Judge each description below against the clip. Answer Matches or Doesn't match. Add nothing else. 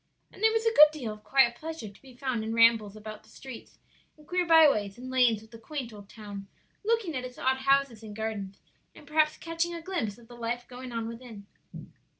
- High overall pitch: Matches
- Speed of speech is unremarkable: Doesn't match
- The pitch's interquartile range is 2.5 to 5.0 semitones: Doesn't match